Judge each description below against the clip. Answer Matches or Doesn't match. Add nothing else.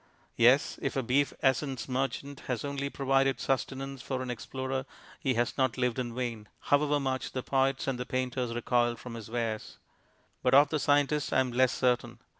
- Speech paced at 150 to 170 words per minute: Doesn't match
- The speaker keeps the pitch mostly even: Matches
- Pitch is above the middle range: Doesn't match